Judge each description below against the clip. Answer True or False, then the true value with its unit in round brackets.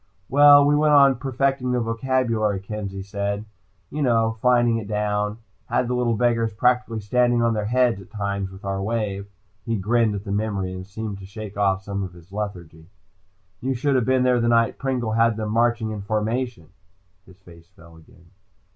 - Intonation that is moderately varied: True (3.7 semitones)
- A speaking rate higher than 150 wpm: True (185 wpm)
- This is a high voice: False (110 Hz)